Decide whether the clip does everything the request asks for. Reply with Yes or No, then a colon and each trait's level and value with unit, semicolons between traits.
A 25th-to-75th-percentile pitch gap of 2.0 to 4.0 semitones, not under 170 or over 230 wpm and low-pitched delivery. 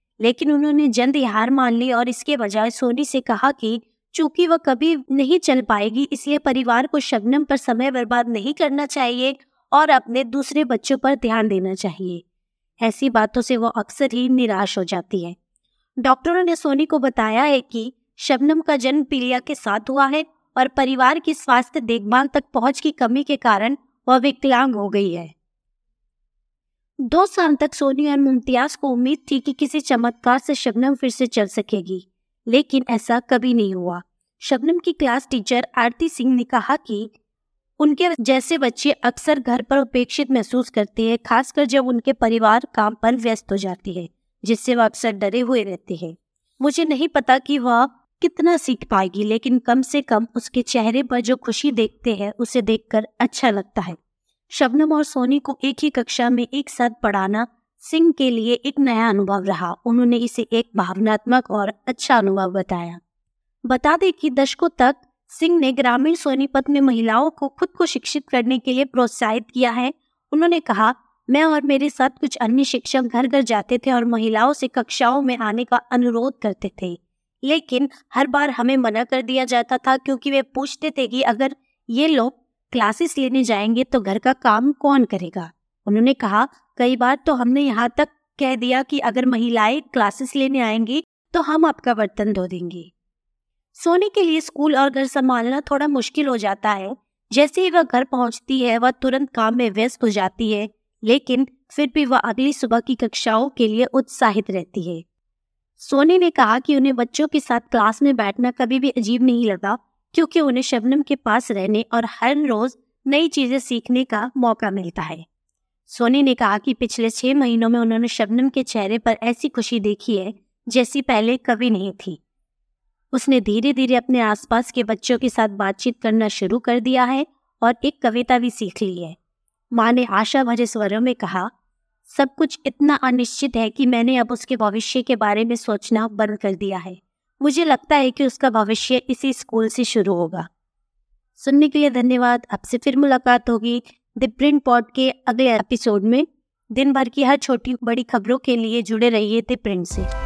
No: average, 3.4 semitones; average, 185 wpm; very high, 250 Hz